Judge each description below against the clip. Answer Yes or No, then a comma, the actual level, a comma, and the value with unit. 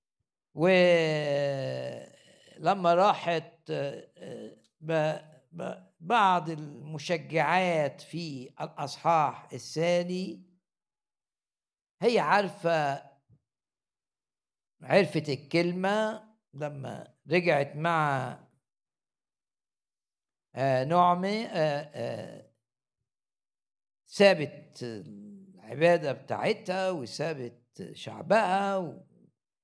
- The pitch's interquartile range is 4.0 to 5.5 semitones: Yes, average, 4.7 semitones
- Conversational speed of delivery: No, slow, 45 wpm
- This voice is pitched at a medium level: Yes, medium, 160 Hz